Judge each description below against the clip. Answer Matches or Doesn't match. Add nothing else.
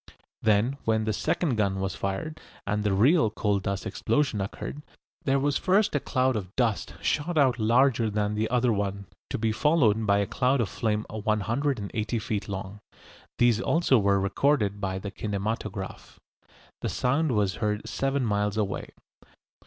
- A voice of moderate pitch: Doesn't match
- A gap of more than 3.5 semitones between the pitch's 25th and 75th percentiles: Matches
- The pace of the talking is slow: Doesn't match